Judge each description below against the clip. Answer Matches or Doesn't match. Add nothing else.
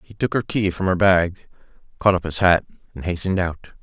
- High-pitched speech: Doesn't match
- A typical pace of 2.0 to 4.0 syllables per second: Doesn't match